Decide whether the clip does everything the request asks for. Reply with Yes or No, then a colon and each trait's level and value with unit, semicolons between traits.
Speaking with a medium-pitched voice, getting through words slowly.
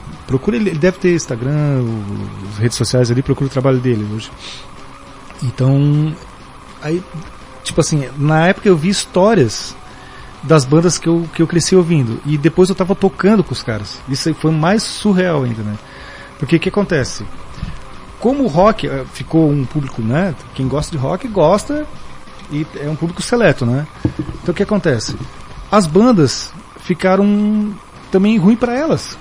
No: medium, 160 Hz; average, 160 wpm